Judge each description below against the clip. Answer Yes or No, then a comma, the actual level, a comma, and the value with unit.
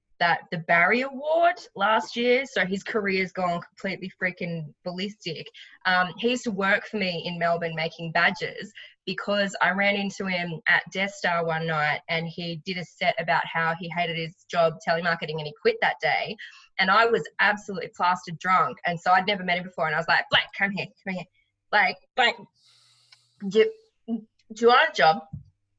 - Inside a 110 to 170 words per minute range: No, average, 190 wpm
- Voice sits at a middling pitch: Yes, medium, 180 Hz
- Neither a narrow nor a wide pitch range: Yes, average, 3.6 semitones